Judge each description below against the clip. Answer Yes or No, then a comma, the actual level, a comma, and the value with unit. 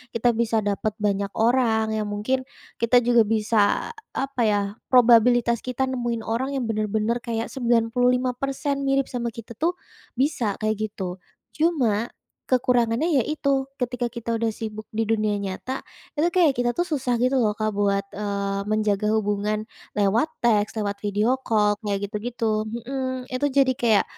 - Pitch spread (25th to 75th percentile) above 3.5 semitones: No, average, 3.1 semitones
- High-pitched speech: Yes, high, 230 Hz